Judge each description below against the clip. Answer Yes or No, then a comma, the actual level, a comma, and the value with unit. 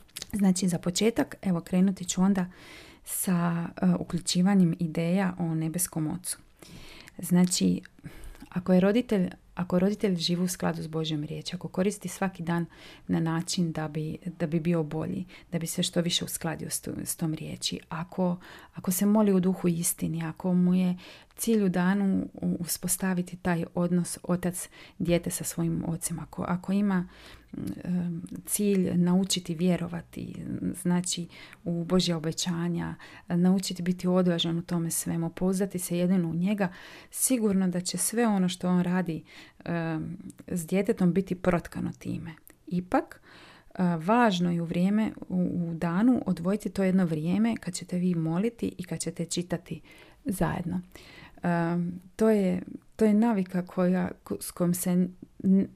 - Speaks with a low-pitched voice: No, medium, 180 Hz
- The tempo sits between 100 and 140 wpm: No, average, 150 wpm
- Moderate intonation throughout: No, narrow, 1.9 semitones